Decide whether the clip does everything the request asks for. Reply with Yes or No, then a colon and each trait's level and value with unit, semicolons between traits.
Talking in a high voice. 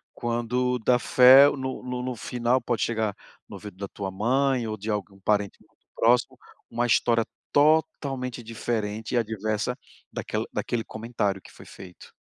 No: low, 115 Hz